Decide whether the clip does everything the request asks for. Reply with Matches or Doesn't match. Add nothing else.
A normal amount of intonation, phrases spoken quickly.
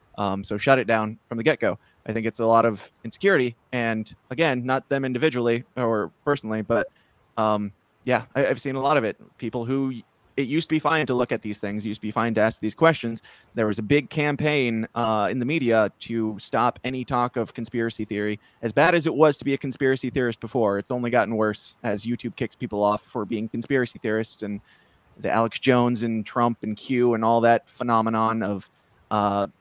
Matches